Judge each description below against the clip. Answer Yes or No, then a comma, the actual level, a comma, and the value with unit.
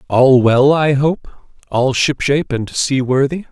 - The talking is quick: No, slow, 135 wpm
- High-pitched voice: No, low, 135 Hz